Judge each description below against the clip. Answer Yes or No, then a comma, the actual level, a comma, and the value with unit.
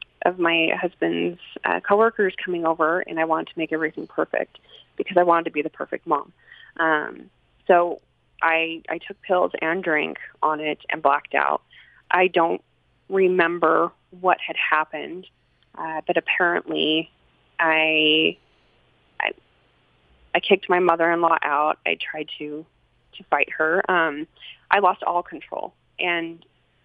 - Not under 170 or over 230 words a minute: No, average, 145 wpm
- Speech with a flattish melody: Yes, narrow, 2.3 semitones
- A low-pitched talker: No, medium, 165 Hz